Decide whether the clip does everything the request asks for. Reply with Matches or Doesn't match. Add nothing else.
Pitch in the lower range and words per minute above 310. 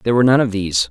Matches